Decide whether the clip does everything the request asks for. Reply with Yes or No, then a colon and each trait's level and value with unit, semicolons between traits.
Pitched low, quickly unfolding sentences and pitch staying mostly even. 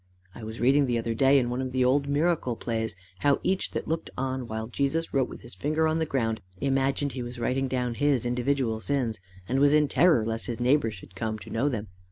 No: low, 130 Hz; fast, 235 wpm; average, 3.6 semitones